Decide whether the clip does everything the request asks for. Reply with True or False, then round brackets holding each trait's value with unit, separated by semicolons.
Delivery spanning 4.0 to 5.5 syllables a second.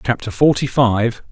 True (4.4 syllables/s)